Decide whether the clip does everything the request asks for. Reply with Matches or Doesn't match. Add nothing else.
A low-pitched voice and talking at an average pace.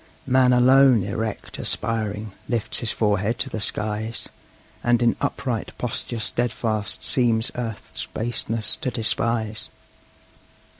Doesn't match